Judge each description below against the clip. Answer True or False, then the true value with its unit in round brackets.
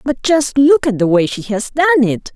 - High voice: True (260 Hz)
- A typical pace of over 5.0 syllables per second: False (4.8 syllables/s)